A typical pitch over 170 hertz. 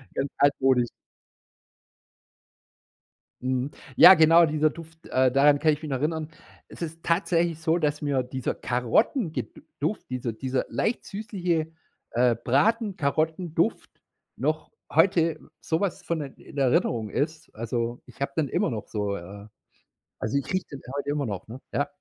No: medium, 145 Hz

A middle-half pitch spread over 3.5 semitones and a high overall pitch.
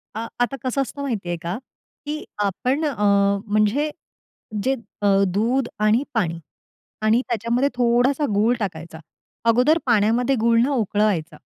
Yes: average, 4.2 semitones; high, 230 Hz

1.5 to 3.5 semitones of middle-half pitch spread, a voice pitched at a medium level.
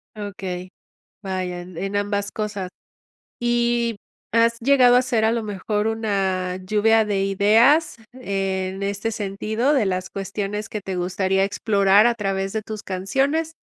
No: average, 2.8 semitones; high, 205 Hz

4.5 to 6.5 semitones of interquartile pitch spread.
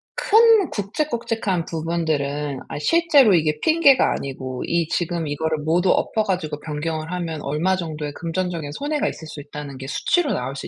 Yes: wide, 5.6 semitones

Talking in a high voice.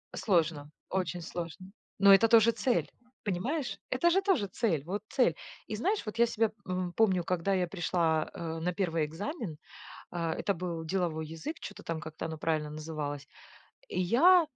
No: medium, 180 Hz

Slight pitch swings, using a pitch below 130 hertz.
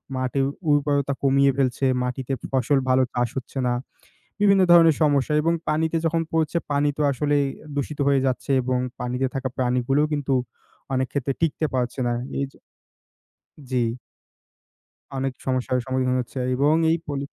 No: narrow, 2.3 semitones; low, 135 Hz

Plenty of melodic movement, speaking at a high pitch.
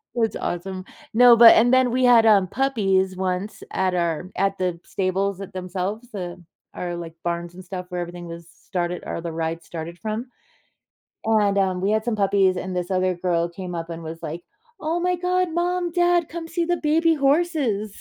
Yes: wide, 5.7 semitones; high, 195 Hz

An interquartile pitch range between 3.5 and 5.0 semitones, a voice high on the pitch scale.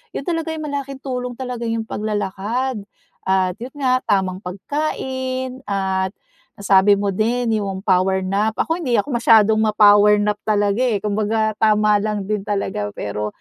Yes: average, 4.1 semitones; high, 215 Hz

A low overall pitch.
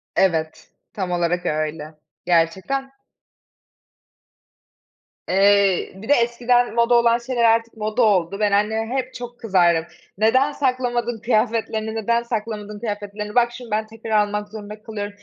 No: high, 220 Hz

